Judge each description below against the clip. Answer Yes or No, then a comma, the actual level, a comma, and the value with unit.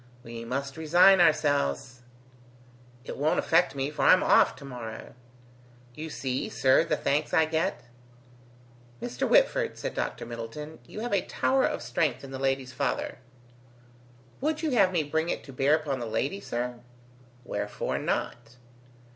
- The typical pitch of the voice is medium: Yes, medium, 145 Hz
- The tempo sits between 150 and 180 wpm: Yes, average, 155 wpm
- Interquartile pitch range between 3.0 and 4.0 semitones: No, average, 4.7 semitones